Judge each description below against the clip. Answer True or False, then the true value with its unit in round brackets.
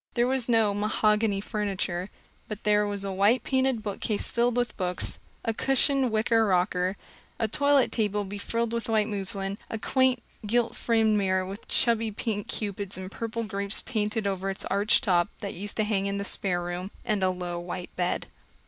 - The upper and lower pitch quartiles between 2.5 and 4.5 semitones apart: True (2.8 semitones)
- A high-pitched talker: True (210 Hz)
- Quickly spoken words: False (180 wpm)